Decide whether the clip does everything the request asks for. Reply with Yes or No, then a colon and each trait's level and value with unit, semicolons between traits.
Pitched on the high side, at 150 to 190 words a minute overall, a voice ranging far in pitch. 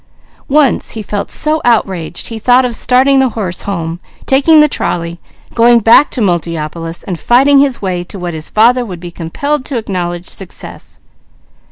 Yes: high, 215 Hz; average, 170 wpm; wide, 6.7 semitones